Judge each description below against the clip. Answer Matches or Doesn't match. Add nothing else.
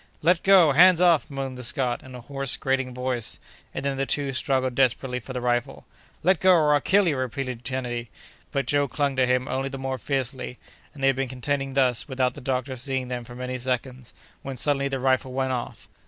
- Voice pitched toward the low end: Matches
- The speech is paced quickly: Matches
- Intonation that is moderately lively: Doesn't match